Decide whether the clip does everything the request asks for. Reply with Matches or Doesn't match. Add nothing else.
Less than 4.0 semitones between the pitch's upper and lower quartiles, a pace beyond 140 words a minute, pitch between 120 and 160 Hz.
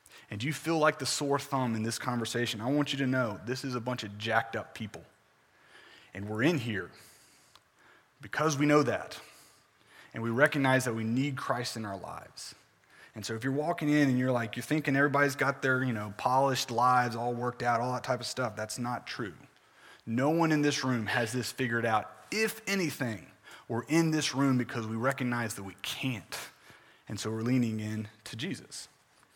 Matches